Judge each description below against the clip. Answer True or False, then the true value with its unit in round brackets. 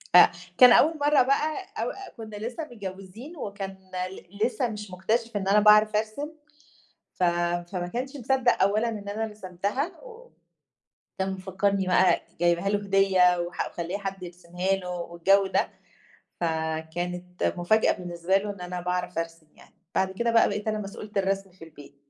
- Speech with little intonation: False (3.5 semitones)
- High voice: True (195 Hz)